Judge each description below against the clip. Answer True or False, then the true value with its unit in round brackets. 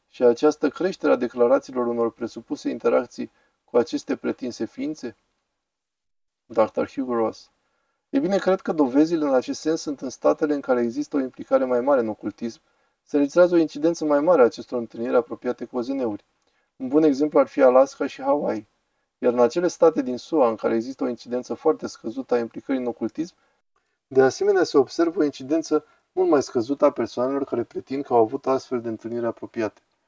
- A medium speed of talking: False (185 wpm)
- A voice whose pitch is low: False (150 Hz)